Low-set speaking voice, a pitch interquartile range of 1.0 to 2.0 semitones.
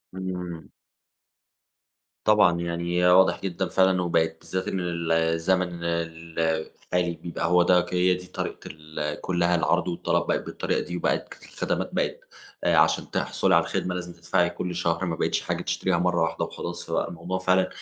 Yes: very low, 85 Hz; narrow, 1.4 semitones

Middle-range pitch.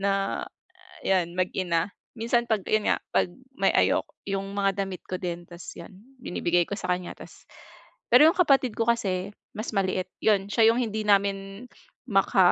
No: high, 195 Hz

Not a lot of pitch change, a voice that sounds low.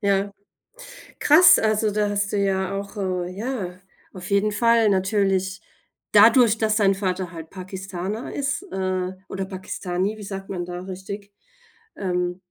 No: narrow, 2.1 semitones; high, 195 Hz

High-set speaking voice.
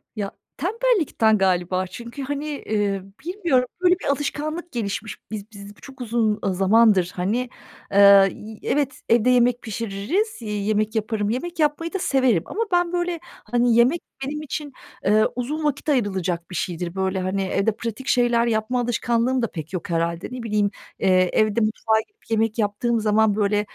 Yes: high, 225 Hz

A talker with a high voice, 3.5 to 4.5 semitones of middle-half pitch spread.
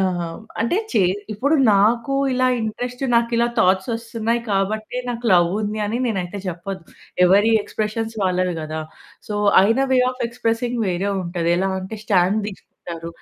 Yes: high, 210 Hz; average, 4.0 semitones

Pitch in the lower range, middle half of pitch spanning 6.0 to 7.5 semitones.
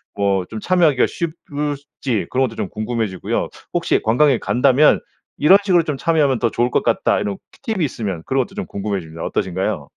Yes: low, 125 Hz; wide, 6.8 semitones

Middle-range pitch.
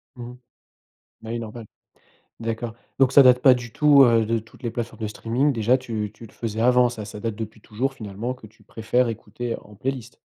No: low, 115 Hz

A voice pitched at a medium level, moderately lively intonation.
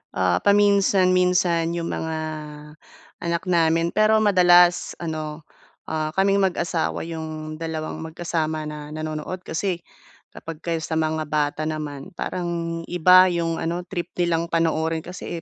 No: medium, 165 Hz; narrow, 2.1 semitones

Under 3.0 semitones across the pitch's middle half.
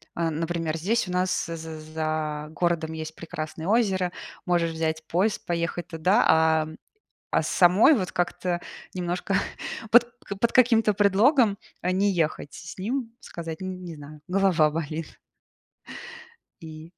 No: average, 3.4 semitones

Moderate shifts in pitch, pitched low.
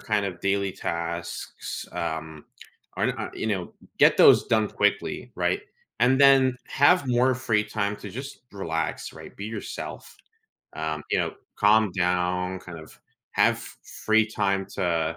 Yes: average, 4.0 semitones; low, 100 Hz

